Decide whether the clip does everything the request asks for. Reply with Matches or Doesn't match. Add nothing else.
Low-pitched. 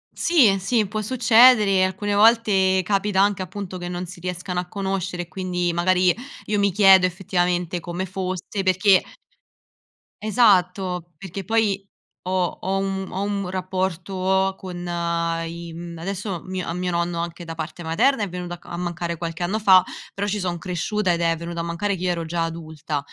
Doesn't match